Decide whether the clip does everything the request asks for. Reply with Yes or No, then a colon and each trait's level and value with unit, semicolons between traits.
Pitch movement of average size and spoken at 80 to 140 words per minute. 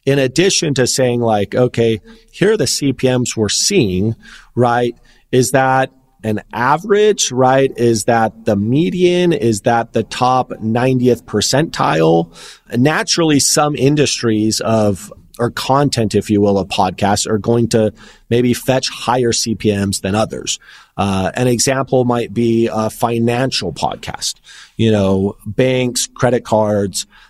Yes: average, 3.1 semitones; slow, 135 wpm